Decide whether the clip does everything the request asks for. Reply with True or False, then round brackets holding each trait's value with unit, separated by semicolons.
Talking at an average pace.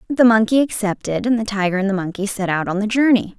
False (250 wpm)